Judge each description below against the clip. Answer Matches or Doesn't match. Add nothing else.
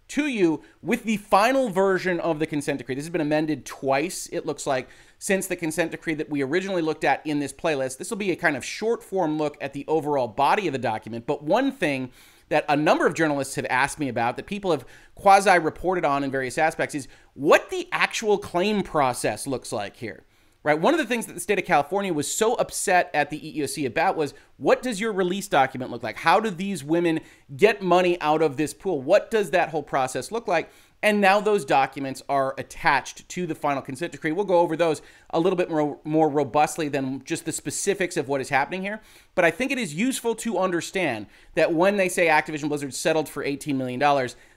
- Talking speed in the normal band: Doesn't match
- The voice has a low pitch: Doesn't match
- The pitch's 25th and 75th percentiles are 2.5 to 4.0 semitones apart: Doesn't match